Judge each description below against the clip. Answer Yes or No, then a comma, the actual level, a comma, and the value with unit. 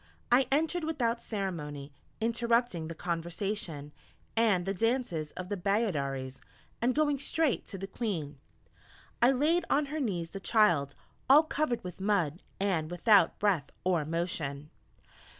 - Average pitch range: No, wide, 6.5 semitones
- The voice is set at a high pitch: Yes, high, 195 Hz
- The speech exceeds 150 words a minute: No, slow, 135 wpm